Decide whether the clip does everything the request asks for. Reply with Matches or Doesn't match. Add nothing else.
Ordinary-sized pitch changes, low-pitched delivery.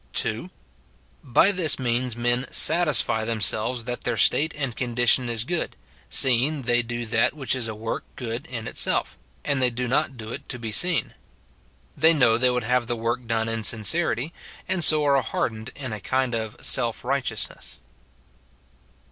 Matches